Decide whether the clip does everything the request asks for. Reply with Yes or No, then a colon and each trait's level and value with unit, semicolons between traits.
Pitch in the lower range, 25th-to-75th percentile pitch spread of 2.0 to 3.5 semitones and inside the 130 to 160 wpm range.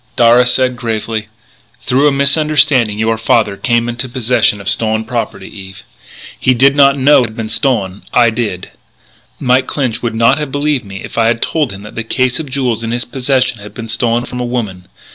No: low, 120 Hz; average, 2.8 semitones; fast, 205 wpm